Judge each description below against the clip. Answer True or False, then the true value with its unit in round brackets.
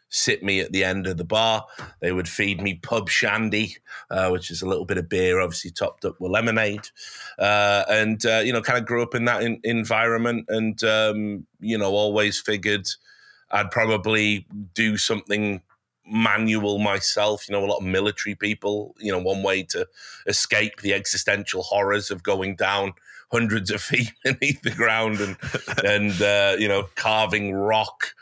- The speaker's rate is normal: True (180 wpm)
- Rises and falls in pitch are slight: True (1.9 semitones)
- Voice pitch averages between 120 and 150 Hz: False (105 Hz)